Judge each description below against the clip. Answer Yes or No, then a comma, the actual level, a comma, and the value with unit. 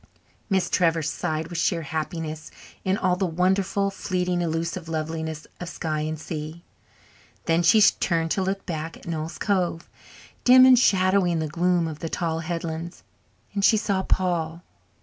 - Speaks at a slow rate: No, average, 160 wpm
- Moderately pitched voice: Yes, medium, 170 Hz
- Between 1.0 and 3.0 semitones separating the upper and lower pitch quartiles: Yes, narrow, 2.6 semitones